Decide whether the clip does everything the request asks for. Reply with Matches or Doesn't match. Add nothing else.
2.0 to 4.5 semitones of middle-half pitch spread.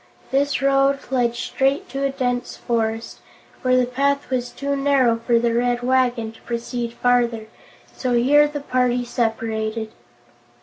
Matches